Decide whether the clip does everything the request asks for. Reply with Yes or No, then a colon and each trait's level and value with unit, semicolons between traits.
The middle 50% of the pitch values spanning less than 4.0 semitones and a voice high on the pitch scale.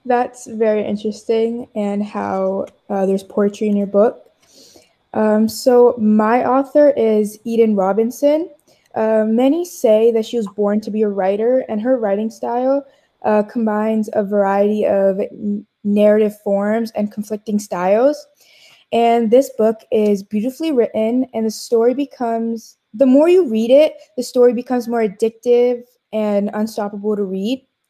Yes: average, 2.9 semitones; high, 220 Hz